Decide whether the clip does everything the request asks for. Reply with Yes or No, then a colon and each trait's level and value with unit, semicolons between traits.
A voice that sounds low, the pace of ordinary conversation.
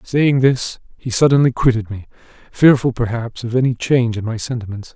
Yes: low, 120 Hz; average, 170 wpm